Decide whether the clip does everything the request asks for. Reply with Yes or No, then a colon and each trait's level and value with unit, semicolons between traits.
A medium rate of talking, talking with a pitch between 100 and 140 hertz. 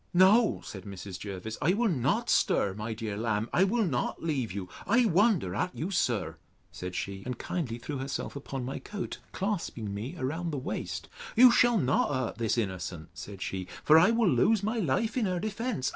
Yes: average, 195 wpm; low, 135 Hz